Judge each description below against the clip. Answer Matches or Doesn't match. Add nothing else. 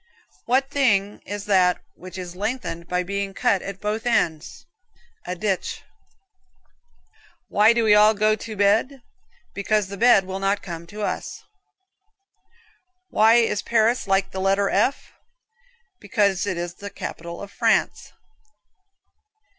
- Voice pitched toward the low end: Doesn't match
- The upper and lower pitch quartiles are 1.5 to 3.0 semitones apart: Matches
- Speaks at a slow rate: Matches